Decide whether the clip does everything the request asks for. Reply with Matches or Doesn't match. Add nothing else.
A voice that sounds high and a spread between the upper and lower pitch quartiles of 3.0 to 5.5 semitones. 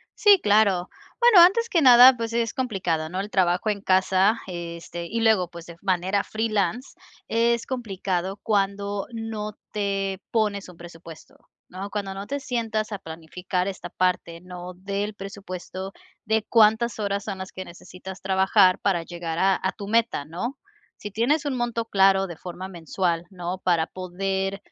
Matches